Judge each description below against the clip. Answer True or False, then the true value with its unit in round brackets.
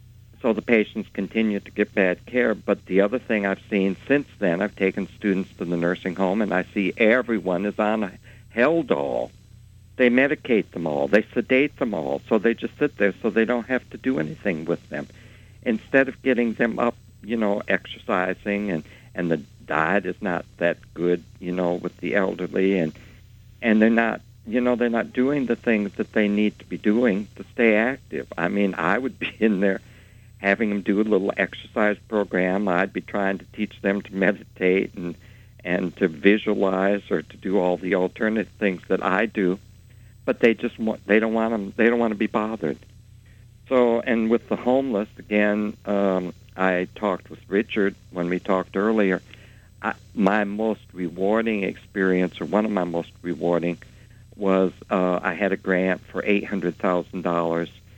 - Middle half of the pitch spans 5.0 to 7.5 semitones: False (3.0 semitones)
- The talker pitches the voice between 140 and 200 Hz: False (105 Hz)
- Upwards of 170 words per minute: True (190 wpm)